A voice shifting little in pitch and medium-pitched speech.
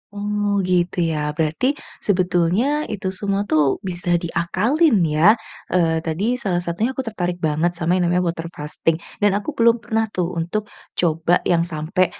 No: average, 3.7 semitones; medium, 175 Hz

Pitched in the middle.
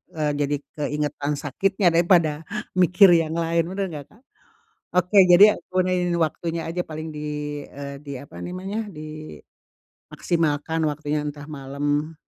Yes: medium, 160 Hz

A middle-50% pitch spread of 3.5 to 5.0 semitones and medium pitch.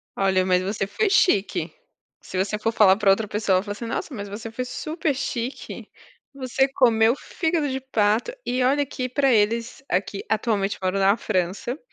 No: average, 4.6 semitones; high, 225 Hz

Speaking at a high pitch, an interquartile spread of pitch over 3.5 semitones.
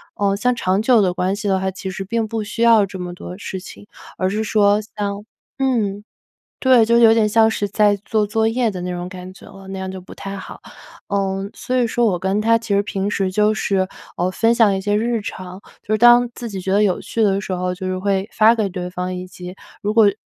No: high, 200 Hz; average, 2.8 semitones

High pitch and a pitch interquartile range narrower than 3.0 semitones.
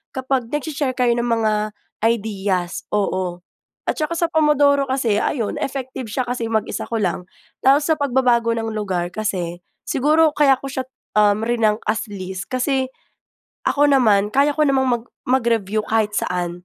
No: high, 235 Hz; average, 4.7 semitones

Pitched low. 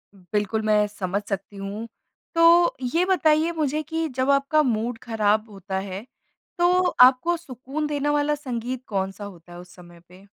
No: high, 230 Hz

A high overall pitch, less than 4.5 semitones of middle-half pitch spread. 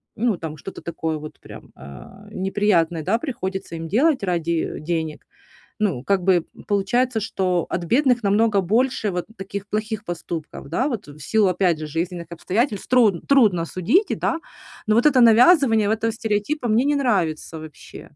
No: high, 195 Hz; average, 5.3 semitones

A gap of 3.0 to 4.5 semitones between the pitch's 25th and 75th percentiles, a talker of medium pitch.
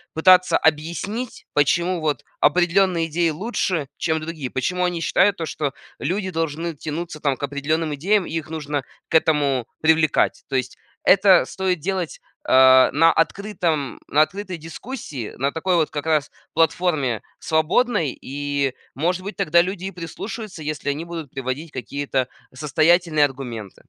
Yes: average, 3.8 semitones; medium, 160 Hz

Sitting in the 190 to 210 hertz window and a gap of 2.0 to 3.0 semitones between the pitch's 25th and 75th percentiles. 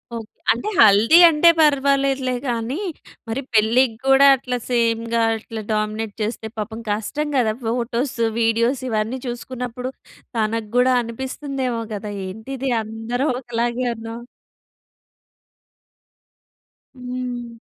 No: high, 235 Hz; narrow, 2.5 semitones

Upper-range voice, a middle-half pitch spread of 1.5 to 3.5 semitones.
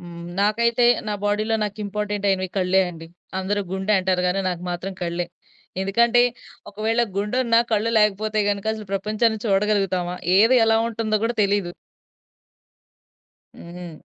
Yes: high, 205 Hz; narrow, 2.5 semitones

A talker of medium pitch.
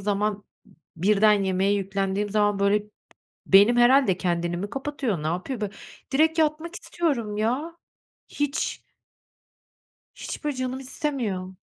No: high, 210 Hz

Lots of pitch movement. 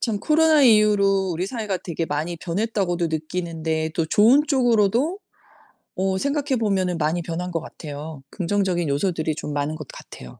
No: average, 4.9 semitones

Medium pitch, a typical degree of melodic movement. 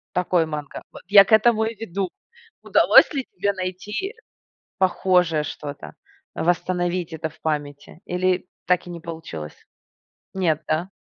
Yes: medium, 180 Hz; average, 3.2 semitones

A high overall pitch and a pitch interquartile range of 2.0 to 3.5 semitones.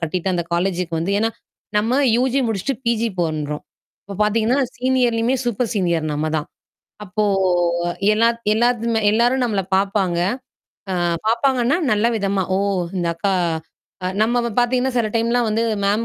No: high, 220 Hz; average, 4.1 semitones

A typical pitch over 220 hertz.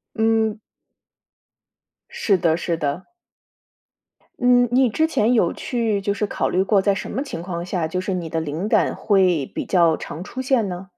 No: high, 195 Hz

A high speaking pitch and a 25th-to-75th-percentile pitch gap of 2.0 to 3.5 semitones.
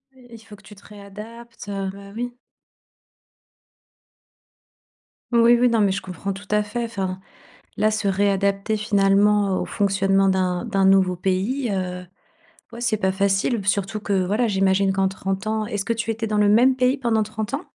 Yes: high, 205 Hz; narrow, 2.6 semitones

